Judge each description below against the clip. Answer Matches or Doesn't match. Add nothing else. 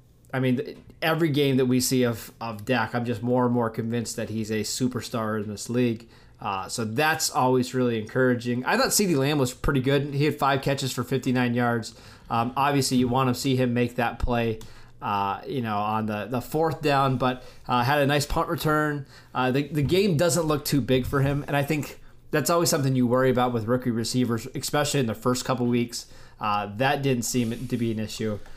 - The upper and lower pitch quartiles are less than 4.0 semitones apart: Matches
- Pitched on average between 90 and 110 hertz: Doesn't match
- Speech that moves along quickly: Matches